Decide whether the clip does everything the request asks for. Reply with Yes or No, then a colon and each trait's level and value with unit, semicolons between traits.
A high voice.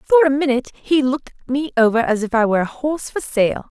Yes: very high, 260 Hz